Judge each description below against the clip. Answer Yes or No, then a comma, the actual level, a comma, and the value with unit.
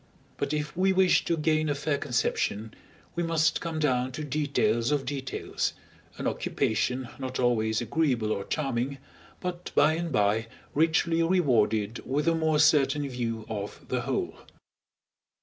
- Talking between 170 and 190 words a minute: No, average, 150 wpm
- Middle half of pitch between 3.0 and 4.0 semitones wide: No, average, 5.2 semitones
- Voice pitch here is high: No, medium, 140 Hz